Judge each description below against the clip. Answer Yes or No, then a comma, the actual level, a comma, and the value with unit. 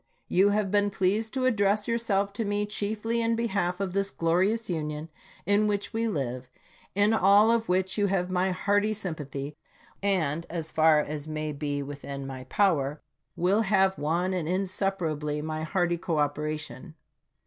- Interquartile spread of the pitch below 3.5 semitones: No, average, 4.9 semitones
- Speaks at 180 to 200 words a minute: No, average, 160 wpm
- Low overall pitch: No, medium, 185 Hz